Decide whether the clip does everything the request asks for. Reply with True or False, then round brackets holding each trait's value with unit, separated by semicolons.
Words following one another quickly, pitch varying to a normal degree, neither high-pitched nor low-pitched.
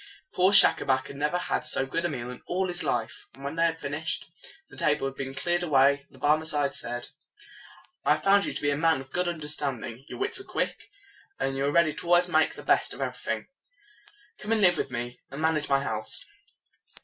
True (235 wpm; 4.2 semitones; 150 Hz)